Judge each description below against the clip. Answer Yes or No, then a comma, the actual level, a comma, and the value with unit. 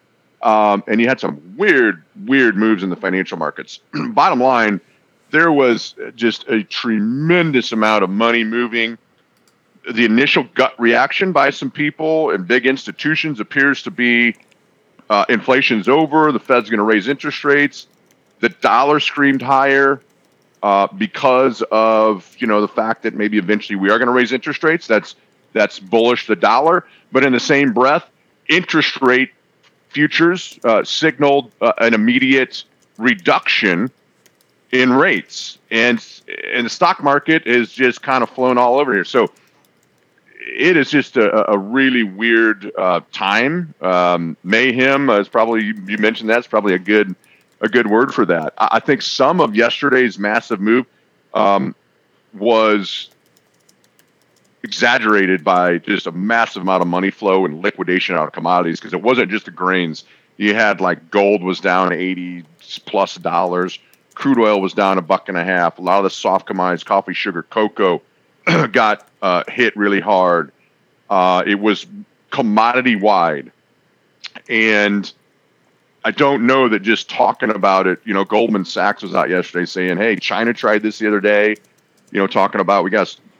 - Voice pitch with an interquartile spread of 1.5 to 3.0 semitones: No, average, 4.4 semitones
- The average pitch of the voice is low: Yes, low, 115 Hz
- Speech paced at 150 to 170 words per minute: Yes, average, 160 wpm